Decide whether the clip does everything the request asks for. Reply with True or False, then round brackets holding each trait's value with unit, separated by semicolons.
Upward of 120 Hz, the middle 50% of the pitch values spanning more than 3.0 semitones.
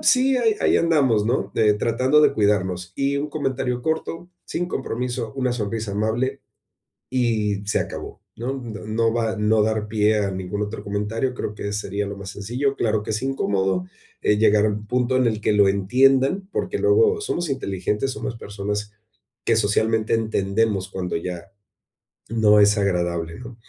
False (110 Hz; 4.0 semitones)